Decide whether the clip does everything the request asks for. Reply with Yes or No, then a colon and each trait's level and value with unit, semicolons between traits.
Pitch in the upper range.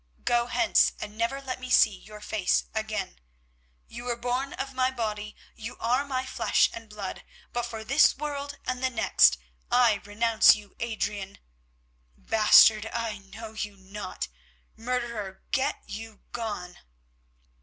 Yes: high, 225 Hz